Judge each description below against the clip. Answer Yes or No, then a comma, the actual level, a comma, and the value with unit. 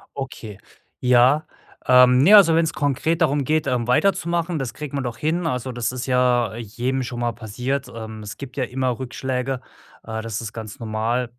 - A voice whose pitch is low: Yes, low, 125 Hz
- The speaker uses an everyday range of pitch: Yes, average, 3.1 semitones